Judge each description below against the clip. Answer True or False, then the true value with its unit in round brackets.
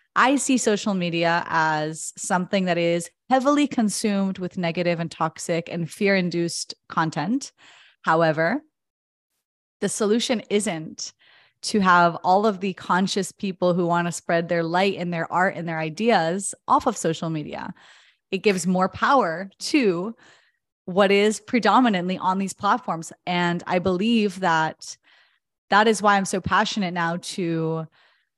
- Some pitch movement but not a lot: True (3.7 semitones)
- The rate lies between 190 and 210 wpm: False (145 wpm)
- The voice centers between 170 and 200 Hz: True (185 Hz)